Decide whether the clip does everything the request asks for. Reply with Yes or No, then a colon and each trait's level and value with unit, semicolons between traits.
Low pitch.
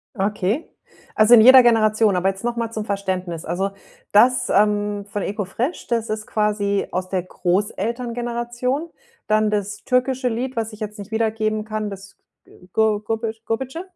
No: high, 215 Hz